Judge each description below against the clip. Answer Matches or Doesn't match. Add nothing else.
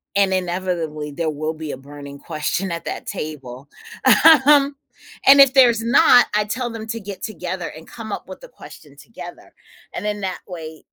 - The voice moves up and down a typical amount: Doesn't match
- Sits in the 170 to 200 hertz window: Matches